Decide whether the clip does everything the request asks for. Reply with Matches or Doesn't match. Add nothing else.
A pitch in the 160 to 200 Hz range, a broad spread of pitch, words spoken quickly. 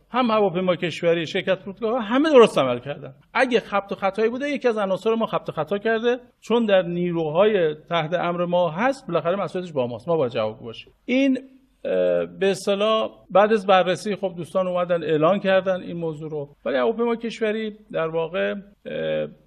Doesn't match